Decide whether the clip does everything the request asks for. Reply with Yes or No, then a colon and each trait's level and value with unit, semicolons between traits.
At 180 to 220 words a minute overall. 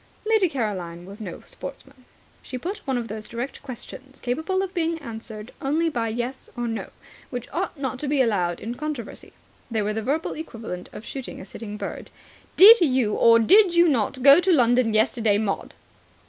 Yes: average, 185 wpm